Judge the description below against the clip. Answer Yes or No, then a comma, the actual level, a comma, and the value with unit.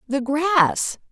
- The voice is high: Yes, very high, 290 Hz